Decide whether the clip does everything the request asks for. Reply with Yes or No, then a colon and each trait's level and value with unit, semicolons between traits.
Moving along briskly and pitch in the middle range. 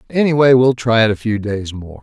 No: fast, 235 wpm; low, 115 Hz